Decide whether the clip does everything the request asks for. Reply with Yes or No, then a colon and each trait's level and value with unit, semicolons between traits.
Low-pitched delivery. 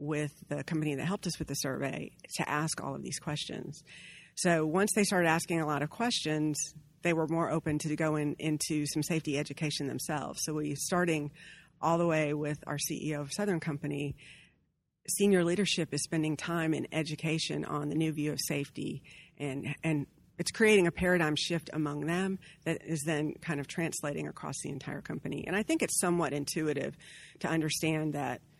No: medium, 155 Hz